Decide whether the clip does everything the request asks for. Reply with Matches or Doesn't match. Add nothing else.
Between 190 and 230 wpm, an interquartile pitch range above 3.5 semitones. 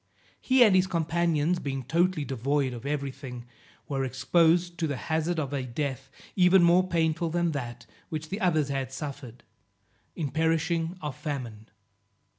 Doesn't match